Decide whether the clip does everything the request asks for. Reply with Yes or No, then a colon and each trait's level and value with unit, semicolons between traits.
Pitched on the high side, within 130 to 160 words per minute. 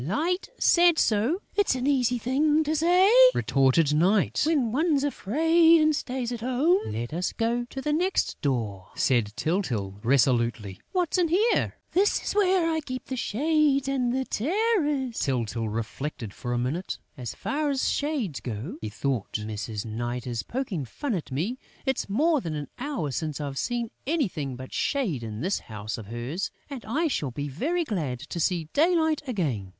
No: high, 225 Hz; average, 175 wpm